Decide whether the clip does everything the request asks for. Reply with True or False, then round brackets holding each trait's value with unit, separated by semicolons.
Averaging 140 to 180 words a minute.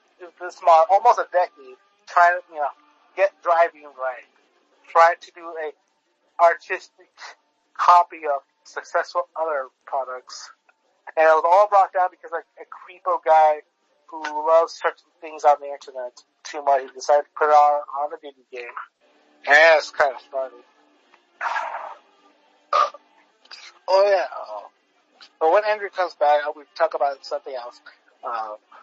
True (150 wpm)